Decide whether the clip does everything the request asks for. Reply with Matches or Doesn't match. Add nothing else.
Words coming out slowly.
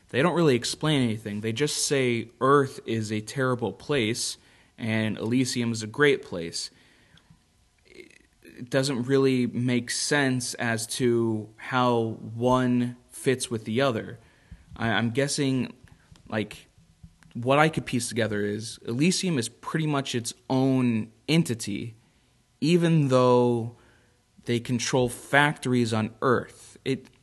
Matches